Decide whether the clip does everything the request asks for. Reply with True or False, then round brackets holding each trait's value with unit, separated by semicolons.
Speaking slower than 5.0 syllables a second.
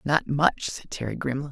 False (5.2 syllables/s)